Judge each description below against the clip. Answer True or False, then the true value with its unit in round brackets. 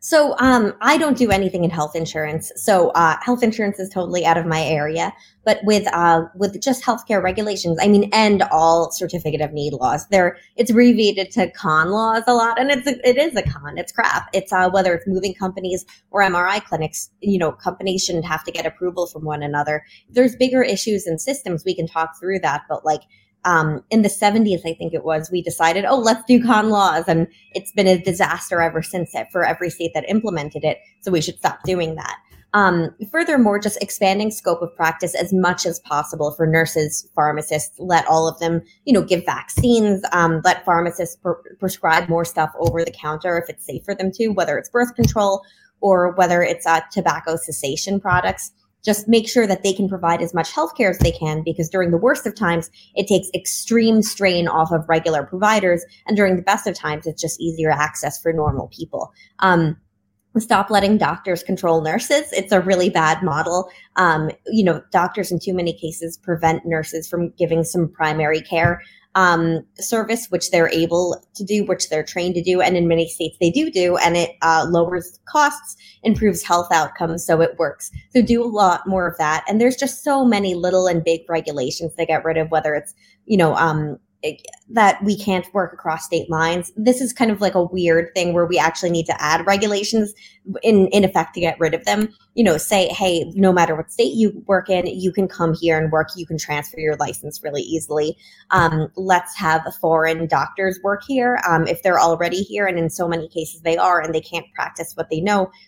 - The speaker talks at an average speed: False (210 wpm)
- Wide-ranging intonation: False (3.6 semitones)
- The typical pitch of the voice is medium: True (180 Hz)